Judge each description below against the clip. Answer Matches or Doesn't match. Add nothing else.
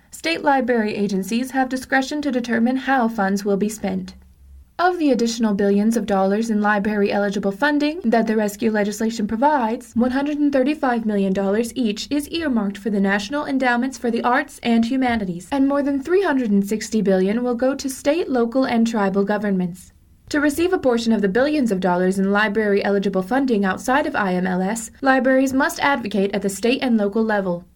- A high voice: Matches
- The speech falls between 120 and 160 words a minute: Doesn't match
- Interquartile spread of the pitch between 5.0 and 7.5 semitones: Doesn't match